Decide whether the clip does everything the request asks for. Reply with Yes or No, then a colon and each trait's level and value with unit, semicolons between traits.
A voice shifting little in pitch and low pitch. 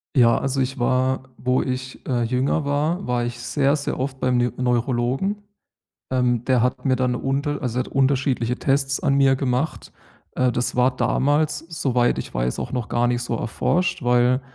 Yes: narrow, 1.9 semitones; low, 130 Hz